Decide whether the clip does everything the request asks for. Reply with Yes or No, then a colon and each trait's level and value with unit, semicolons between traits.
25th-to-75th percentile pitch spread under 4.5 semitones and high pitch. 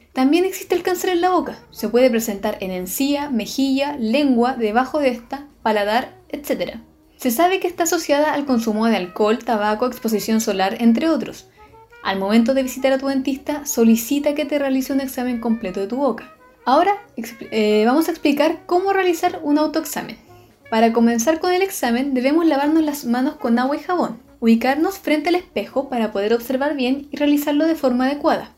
No: average, 5.0 semitones; very high, 270 Hz